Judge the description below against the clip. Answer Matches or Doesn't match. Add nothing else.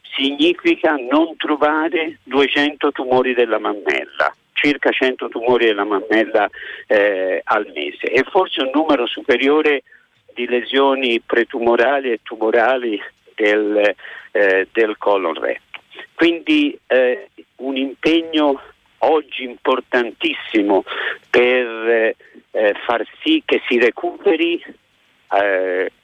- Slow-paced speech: Matches